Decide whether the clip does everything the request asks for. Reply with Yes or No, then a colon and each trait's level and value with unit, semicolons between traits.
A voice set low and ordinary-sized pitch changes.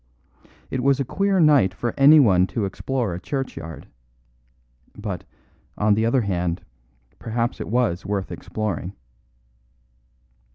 No: low, 110 Hz; wide, 5.8 semitones